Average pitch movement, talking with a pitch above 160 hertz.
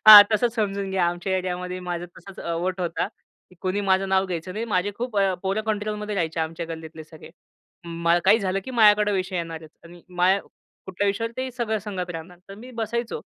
Yes: average, 3.1 semitones; high, 190 Hz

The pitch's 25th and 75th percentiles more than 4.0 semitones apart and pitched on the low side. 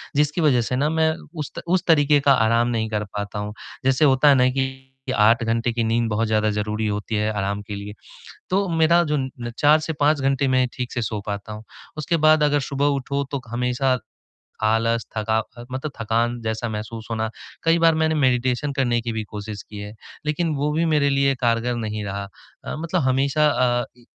Yes: average, 4.7 semitones; low, 125 Hz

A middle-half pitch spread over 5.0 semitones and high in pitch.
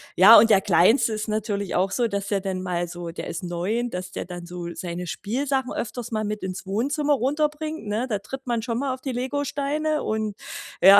Yes: wide, 5.6 semitones; high, 215 Hz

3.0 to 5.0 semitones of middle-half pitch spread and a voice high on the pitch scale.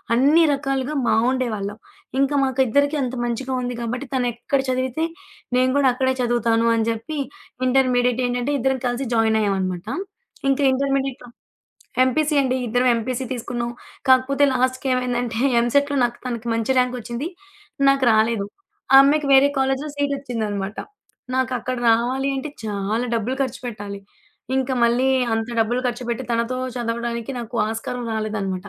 No: narrow, 2.6 semitones; high, 245 Hz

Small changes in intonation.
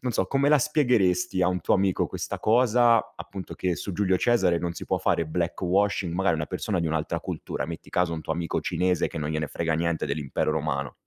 No: average, 3.7 semitones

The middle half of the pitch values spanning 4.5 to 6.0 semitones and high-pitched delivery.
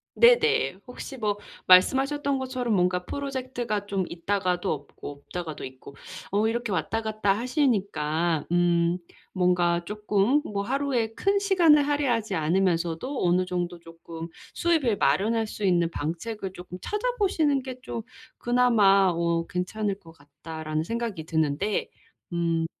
No: wide, 6.4 semitones; high, 200 Hz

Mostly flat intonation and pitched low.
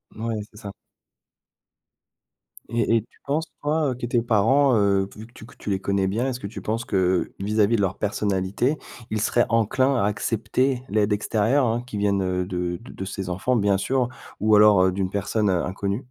No: average, 3.5 semitones; low, 105 Hz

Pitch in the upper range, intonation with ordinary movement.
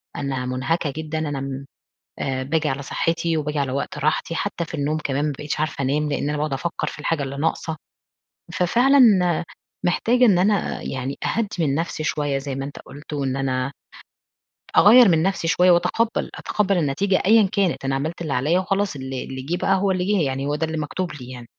No: medium, 150 Hz; average, 4.6 semitones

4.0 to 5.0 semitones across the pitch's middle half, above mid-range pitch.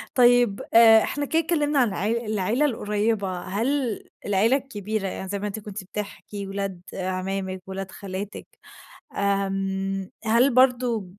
No: average, 3.6 semitones; high, 205 Hz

